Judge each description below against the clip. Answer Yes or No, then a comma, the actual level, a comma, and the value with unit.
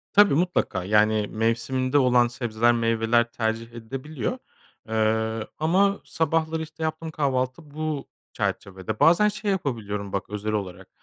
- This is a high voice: No, low, 120 Hz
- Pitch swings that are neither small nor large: No, wide, 6.2 semitones